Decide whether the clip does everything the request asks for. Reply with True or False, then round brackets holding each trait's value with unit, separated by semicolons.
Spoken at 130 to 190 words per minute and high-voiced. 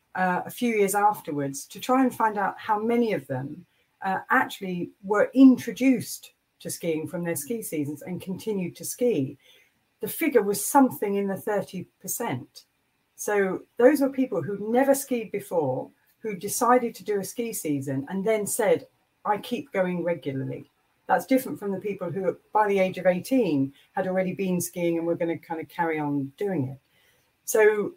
True (180 wpm; 195 Hz)